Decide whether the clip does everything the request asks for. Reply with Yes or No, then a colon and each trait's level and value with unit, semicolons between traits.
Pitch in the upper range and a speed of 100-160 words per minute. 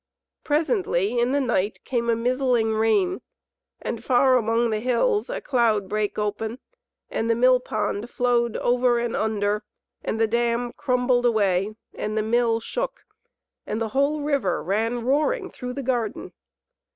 Yes: high, 235 Hz; average, 150 wpm